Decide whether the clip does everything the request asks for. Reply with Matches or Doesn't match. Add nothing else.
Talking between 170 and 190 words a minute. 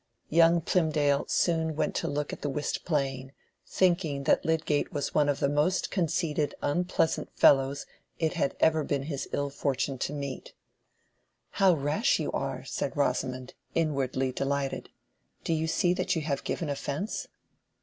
Doesn't match